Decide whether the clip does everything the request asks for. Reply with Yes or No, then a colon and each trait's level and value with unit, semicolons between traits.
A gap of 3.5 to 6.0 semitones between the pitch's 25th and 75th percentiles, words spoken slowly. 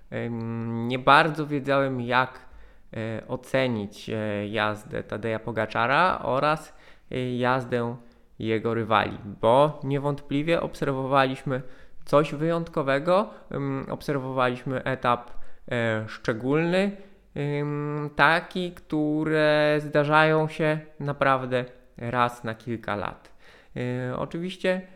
Yes: average, 4.2 semitones; slow, 70 wpm